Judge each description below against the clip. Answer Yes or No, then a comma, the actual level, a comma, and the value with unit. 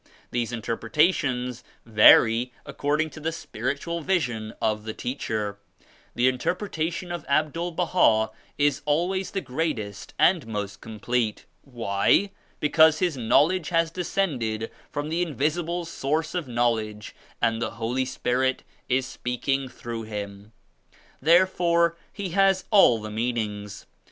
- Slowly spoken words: Yes, slow, 125 wpm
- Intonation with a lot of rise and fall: Yes, wide, 6.8 semitones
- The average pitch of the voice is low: Yes, low, 130 Hz